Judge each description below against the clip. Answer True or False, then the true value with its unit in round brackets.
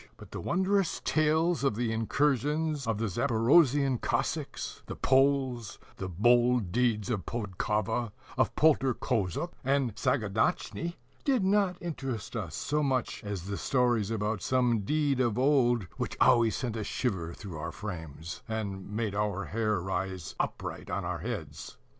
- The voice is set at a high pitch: False (120 Hz)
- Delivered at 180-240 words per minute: False (145 wpm)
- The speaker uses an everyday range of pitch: True (5.0 semitones)